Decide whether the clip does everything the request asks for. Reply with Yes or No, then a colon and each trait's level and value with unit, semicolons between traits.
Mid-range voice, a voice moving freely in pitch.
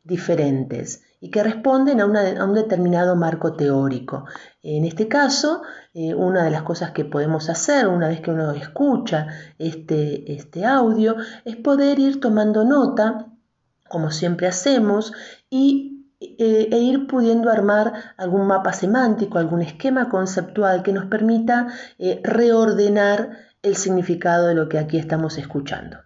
No: high, 200 Hz; wide, 5.9 semitones